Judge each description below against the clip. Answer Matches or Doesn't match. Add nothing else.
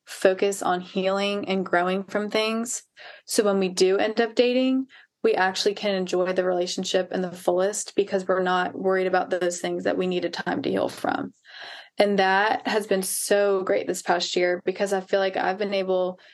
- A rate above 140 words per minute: Matches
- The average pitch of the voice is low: Doesn't match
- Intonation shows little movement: Matches